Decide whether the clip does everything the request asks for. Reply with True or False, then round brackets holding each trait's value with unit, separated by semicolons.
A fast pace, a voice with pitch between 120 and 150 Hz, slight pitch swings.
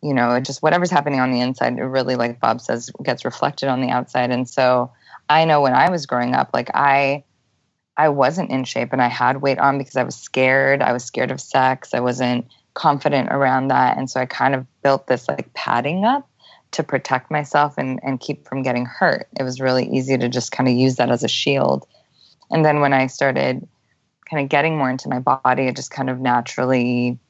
True (225 wpm; 130 Hz; 1.9 semitones)